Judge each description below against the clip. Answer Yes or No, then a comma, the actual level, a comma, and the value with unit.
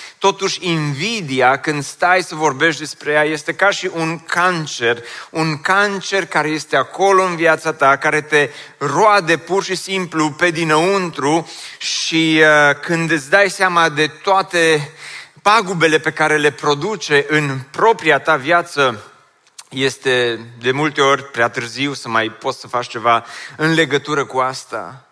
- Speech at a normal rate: Yes, average, 150 wpm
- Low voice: No, medium, 155 Hz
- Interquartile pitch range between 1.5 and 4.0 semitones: Yes, average, 3.4 semitones